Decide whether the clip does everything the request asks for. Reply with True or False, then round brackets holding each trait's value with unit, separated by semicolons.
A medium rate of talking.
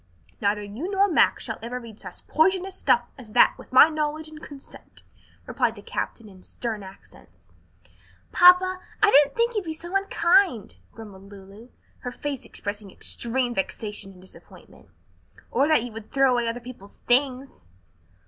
True (160 wpm)